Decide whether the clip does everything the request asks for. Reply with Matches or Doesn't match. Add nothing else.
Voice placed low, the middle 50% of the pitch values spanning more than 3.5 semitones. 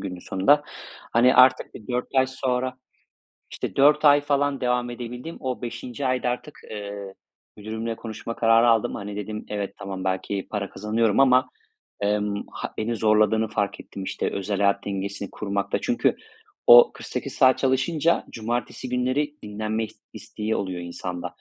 Matches